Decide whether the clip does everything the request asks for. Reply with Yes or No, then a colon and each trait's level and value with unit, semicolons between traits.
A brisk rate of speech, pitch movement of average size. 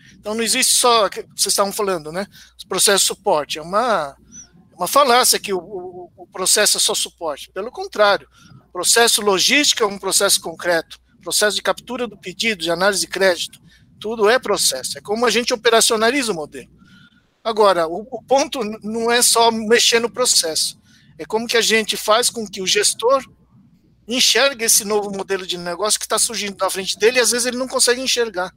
Yes: fast, 190 wpm; average, 3.7 semitones